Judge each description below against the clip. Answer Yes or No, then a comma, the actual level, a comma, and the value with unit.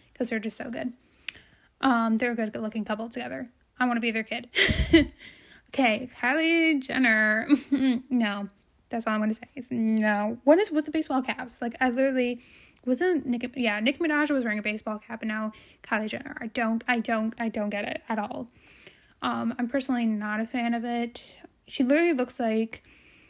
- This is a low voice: No, high, 240 Hz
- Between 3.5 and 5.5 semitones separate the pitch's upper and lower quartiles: No, average, 2.9 semitones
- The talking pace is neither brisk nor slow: Yes, average, 190 wpm